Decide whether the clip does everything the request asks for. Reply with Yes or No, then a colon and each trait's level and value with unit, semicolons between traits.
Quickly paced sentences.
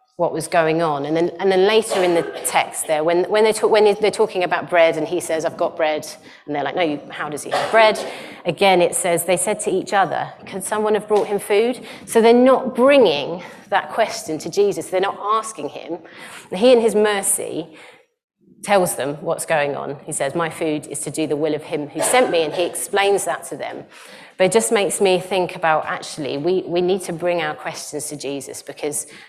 Yes: fast, 230 wpm